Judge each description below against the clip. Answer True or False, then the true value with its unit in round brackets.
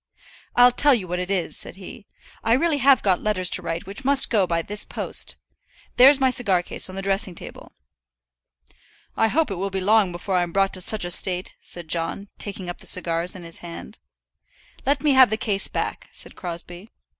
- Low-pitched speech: False (195 Hz)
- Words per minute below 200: False (205 wpm)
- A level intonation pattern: False (4.3 semitones)